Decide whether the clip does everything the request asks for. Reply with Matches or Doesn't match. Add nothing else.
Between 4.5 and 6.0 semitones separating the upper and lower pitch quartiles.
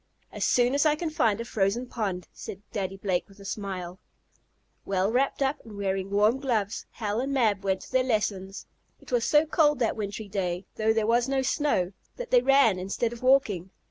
Matches